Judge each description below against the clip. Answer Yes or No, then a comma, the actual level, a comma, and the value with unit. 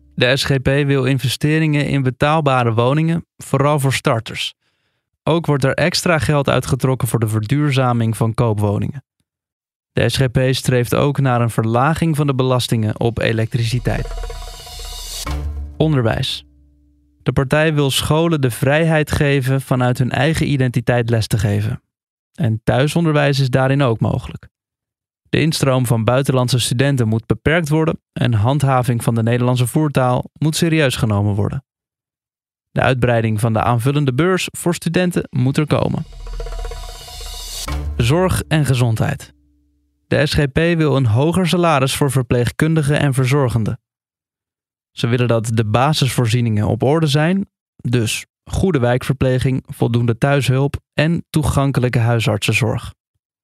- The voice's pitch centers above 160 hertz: No, low, 130 Hz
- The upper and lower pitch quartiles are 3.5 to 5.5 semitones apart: Yes, average, 3.9 semitones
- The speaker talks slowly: Yes, slow, 125 wpm